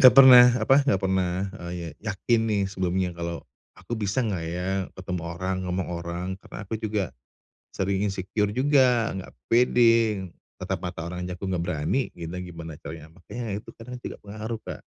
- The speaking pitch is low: Yes, very low, 95 Hz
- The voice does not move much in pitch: No, average, 4.2 semitones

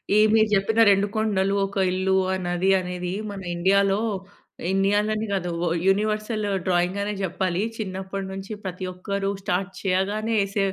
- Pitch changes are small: Yes, narrow, 1.7 semitones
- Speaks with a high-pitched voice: Yes, high, 195 Hz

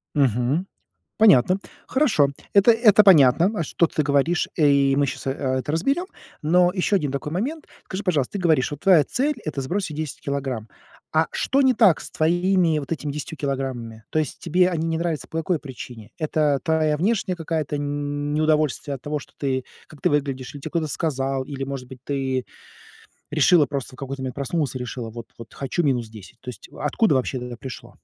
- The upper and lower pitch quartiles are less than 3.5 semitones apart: No, average, 4.3 semitones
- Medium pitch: Yes, medium, 150 Hz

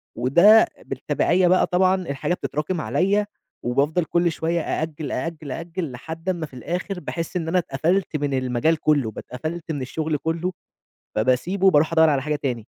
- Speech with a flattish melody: No, average, 4.0 semitones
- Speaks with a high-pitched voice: No, medium, 160 Hz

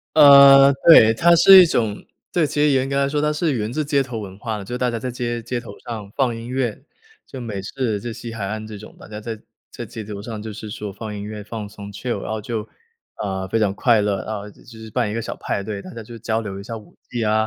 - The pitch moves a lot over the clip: No, average, 3.2 semitones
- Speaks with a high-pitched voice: No, low, 115 Hz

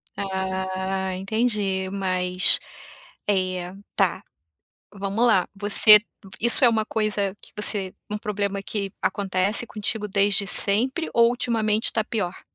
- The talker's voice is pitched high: Yes, high, 200 Hz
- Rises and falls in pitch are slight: Yes, narrow, 2.2 semitones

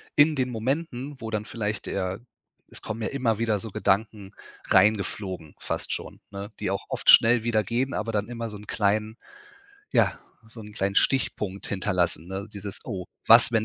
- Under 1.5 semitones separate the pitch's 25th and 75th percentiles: No, average, 2.7 semitones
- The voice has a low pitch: Yes, low, 110 Hz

